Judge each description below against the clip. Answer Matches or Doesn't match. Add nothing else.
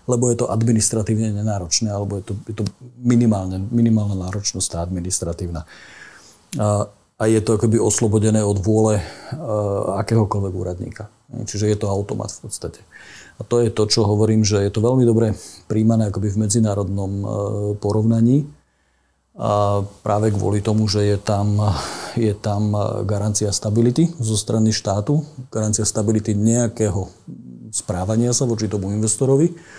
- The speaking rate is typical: Matches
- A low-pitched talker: Matches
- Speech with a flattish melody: Matches